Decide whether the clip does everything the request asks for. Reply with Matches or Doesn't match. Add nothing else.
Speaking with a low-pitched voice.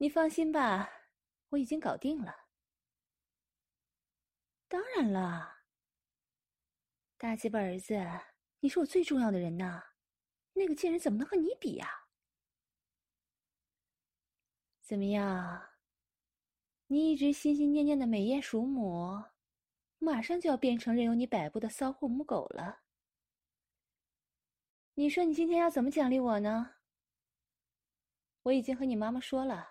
Doesn't match